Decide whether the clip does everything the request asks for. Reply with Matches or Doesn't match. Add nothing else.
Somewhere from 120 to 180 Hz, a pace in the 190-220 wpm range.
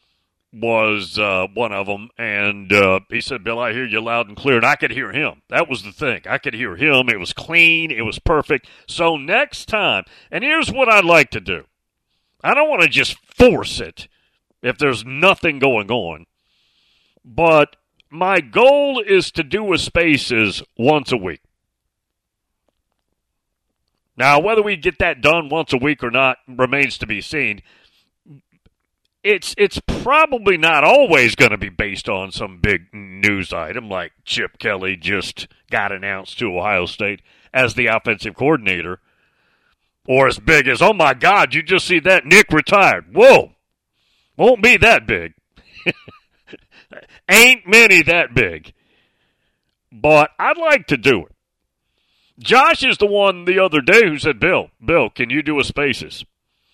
Doesn't match